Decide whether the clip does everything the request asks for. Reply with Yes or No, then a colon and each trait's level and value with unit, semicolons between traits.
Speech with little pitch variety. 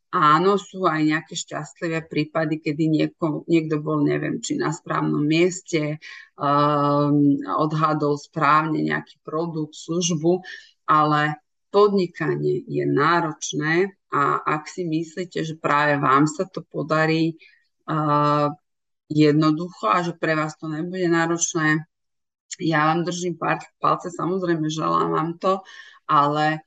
Yes: narrow, 2.3 semitones